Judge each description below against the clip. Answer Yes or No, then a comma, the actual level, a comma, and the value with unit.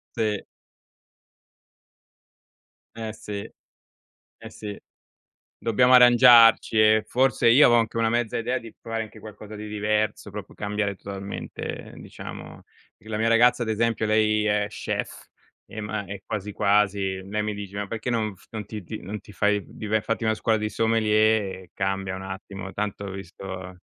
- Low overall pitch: Yes, low, 105 Hz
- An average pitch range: No, narrow, 1.9 semitones